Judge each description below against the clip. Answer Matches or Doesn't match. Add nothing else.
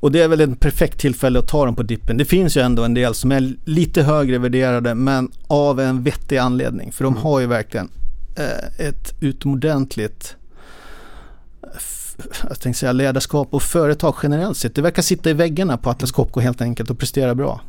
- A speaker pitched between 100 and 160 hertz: Matches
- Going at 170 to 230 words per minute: Matches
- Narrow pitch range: Doesn't match